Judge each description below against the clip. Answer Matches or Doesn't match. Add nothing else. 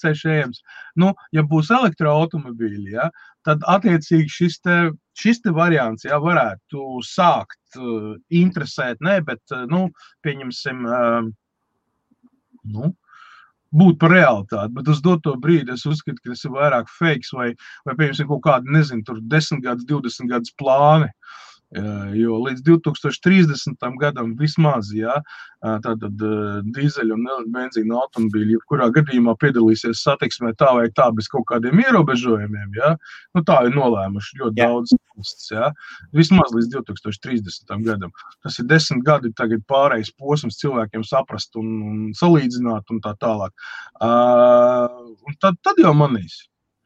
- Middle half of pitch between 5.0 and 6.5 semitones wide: Matches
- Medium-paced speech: Doesn't match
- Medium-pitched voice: Doesn't match